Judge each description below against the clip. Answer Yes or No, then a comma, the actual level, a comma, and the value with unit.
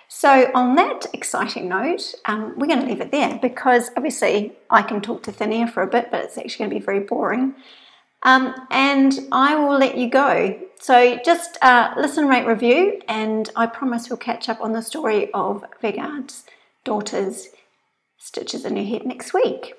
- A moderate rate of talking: Yes, average, 190 wpm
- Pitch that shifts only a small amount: No, average, 3.4 semitones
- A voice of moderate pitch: No, very high, 255 Hz